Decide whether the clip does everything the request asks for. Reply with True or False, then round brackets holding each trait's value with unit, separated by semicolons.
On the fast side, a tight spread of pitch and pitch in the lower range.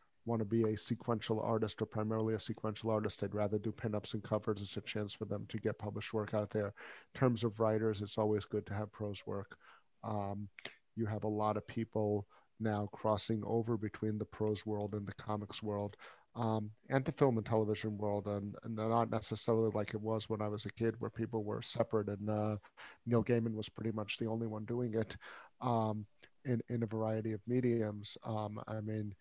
True (210 wpm; 1.3 semitones; 110 Hz)